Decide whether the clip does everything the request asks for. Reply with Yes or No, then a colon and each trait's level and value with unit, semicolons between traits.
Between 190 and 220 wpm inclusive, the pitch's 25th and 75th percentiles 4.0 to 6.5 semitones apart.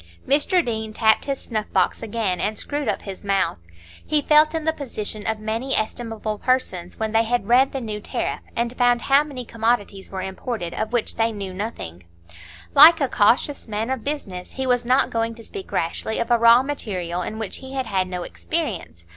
Yes: average, 200 wpm; average, 4.3 semitones